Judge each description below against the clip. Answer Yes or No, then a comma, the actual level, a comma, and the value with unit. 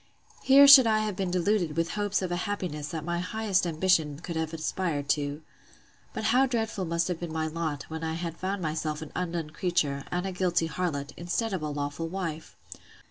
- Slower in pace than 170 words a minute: No, fast, 205 wpm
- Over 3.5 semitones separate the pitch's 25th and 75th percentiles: No, average, 3.2 semitones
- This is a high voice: No, medium, 170 Hz